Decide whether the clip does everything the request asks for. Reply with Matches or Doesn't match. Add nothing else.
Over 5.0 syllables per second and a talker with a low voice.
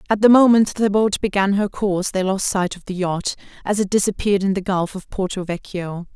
Doesn't match